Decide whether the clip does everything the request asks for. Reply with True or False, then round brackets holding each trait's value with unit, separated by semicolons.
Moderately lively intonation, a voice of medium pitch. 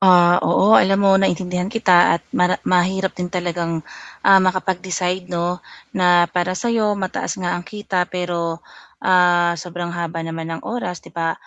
False (1.3 semitones; 180 Hz)